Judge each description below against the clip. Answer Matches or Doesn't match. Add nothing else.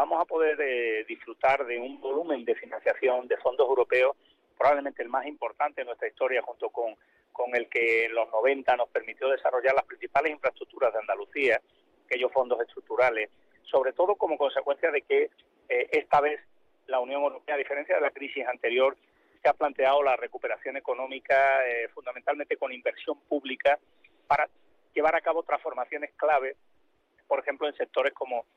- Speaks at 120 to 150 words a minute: Doesn't match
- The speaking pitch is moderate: Matches